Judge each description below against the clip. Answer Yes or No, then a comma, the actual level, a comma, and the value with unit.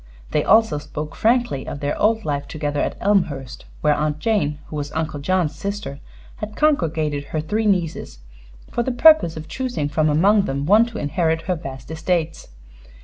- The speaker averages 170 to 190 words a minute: Yes, average, 175 wpm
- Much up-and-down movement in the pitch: Yes, wide, 6.0 semitones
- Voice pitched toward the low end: No, medium, 160 Hz